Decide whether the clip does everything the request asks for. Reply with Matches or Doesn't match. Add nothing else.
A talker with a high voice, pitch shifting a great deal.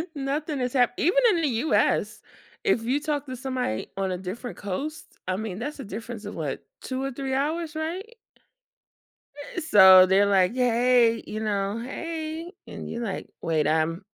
Matches